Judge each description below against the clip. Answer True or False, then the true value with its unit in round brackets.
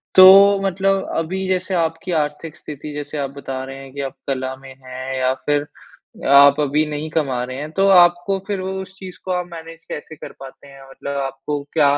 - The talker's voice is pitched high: False (150 Hz)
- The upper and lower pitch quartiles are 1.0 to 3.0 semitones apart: False (5.0 semitones)